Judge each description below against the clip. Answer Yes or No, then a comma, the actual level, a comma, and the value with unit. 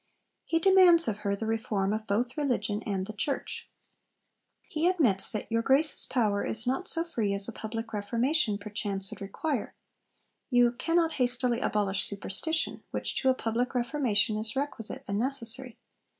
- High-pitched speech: Yes, high, 230 Hz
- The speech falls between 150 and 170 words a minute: Yes, average, 160 wpm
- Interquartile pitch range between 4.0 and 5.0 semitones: Yes, average, 4.6 semitones